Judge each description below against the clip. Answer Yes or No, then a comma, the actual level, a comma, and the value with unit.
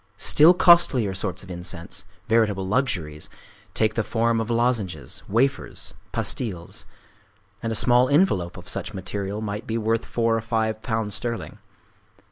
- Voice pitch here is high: No, low, 110 Hz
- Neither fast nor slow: No, slow, 130 wpm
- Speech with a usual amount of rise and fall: Yes, average, 3.4 semitones